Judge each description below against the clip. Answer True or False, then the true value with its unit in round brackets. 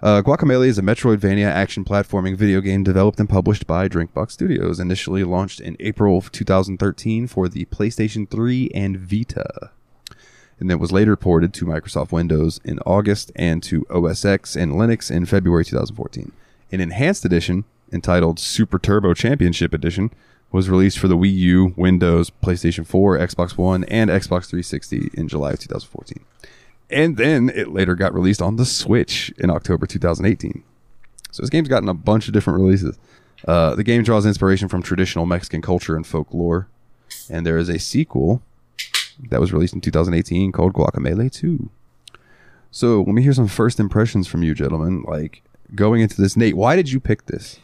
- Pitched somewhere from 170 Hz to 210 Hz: False (95 Hz)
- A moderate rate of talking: True (170 wpm)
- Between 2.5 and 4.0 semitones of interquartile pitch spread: True (3.6 semitones)